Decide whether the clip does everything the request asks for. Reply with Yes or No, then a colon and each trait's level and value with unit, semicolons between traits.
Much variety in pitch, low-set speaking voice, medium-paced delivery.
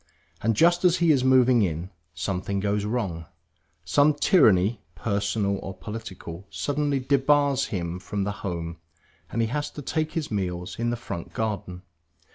Yes: wide, 6.3 semitones; low, 105 Hz; average, 155 wpm